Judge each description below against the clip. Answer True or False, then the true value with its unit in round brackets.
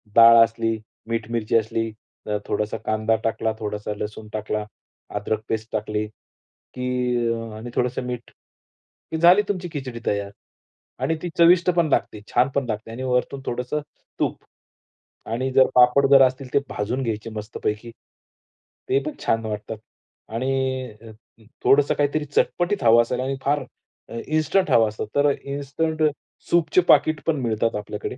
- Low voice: True (125 Hz)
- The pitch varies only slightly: False (4.3 semitones)